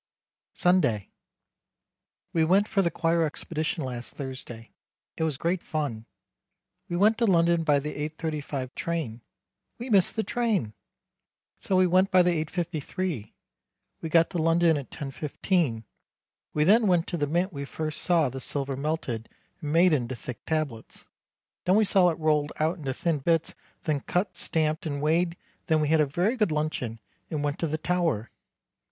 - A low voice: No, medium, 160 Hz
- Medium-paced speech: Yes, average, 165 wpm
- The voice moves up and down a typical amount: Yes, average, 3.7 semitones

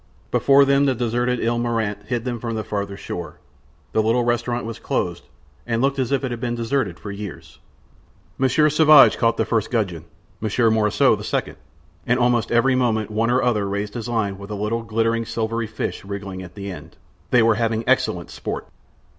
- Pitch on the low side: Yes, low, 115 Hz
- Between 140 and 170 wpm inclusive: No, average, 195 wpm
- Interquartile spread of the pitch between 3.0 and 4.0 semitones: No, narrow, 2.5 semitones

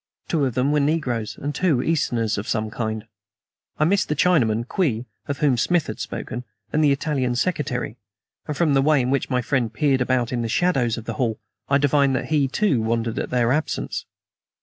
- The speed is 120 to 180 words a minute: No, average, 200 wpm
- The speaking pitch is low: Yes, low, 130 Hz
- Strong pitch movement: No, average, 4.1 semitones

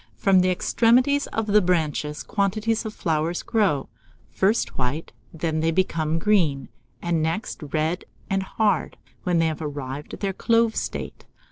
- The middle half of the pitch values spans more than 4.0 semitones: Yes, average, 5.2 semitones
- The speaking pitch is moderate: Yes, medium, 180 Hz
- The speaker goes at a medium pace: Yes, average, 150 wpm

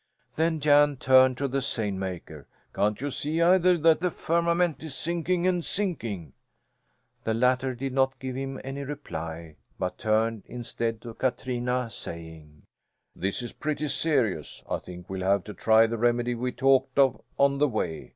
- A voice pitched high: No, low, 130 Hz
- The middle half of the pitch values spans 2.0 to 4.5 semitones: No, average, 5.2 semitones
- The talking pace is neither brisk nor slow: Yes, average, 165 wpm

